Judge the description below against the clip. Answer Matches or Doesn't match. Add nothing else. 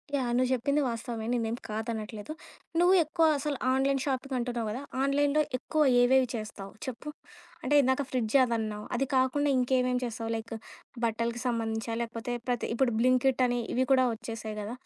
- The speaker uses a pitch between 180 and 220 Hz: Doesn't match